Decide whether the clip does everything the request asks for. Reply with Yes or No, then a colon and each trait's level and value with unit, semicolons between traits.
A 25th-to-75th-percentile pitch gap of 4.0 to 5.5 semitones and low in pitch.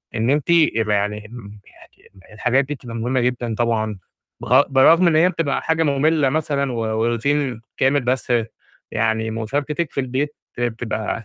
Yes: average, 4.3 semitones; low, 125 Hz